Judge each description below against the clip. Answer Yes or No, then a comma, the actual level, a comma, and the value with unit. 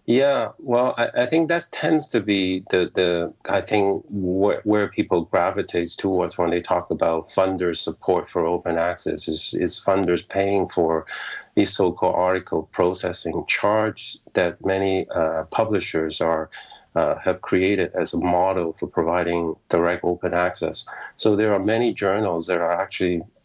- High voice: No, very low, 95 Hz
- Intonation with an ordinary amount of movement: Yes, average, 3.4 semitones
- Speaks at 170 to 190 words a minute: No, average, 155 wpm